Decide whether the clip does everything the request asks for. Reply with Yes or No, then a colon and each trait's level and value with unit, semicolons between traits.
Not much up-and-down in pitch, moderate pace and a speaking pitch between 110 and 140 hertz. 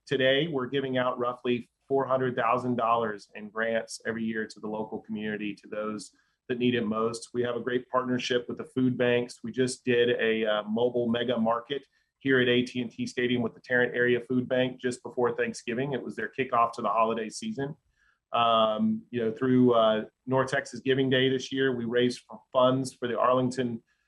Yes: narrow, 2.0 semitones; average, 185 wpm; low, 120 Hz